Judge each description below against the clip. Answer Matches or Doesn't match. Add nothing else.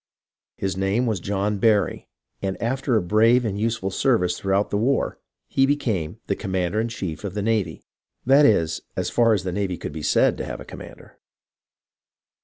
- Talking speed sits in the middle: Matches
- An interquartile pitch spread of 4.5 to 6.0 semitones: Doesn't match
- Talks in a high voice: Doesn't match